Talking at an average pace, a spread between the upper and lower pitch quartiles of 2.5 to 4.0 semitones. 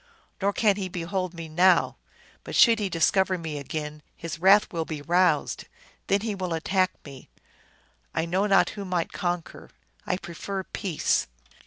Yes: average, 160 wpm; average, 2.9 semitones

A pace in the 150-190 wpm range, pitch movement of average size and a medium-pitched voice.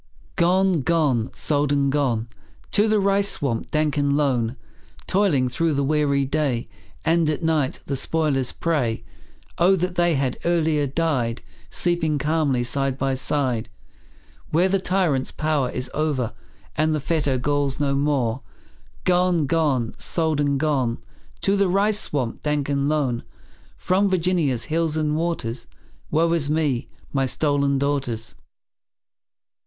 No: average, 140 wpm; average, 3.7 semitones; medium, 145 Hz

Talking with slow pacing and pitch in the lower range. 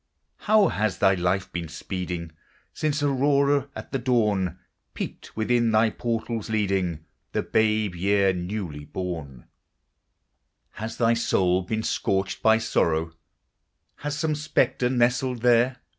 Yes: slow, 125 wpm; low, 110 Hz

